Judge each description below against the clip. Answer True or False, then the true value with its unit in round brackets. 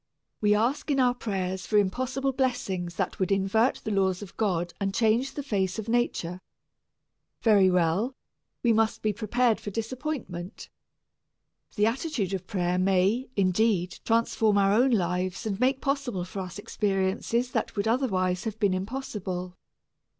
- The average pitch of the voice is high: True (210 Hz)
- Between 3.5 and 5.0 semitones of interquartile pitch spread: True (4.3 semitones)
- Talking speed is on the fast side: False (150 wpm)